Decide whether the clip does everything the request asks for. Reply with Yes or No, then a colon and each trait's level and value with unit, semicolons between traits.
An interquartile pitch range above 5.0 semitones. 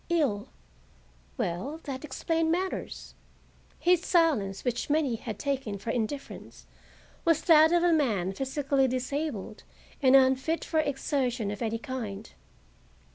Yes: wide, 5.6 semitones